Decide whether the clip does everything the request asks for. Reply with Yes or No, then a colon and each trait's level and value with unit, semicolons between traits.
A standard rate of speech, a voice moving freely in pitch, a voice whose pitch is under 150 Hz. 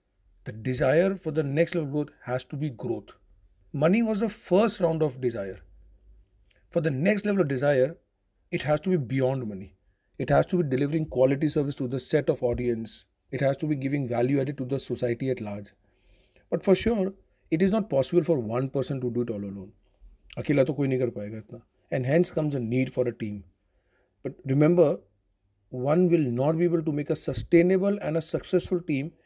Yes: average, 190 wpm; wide, 6.1 semitones; low, 135 Hz